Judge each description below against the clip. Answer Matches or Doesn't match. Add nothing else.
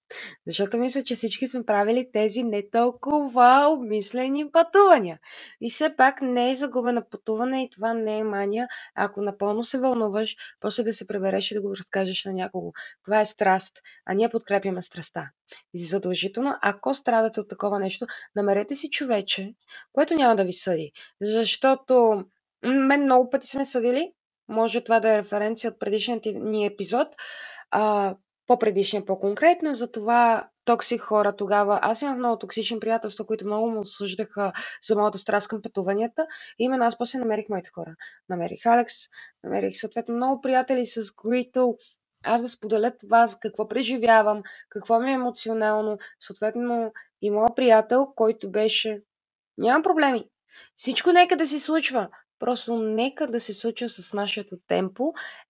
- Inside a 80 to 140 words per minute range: Doesn't match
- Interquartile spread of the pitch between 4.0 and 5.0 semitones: Doesn't match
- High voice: Matches